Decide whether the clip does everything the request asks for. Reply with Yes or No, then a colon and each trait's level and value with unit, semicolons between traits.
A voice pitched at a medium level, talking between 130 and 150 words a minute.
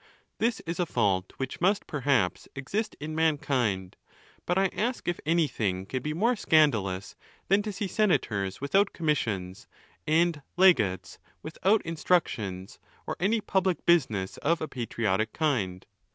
Yes: medium, 150 Hz; average, 140 wpm